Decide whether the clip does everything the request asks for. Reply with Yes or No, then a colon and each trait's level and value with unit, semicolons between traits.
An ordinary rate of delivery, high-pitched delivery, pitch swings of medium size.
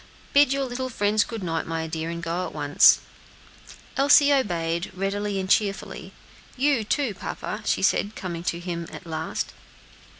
No: average, 155 wpm; high, 195 Hz; wide, 6.5 semitones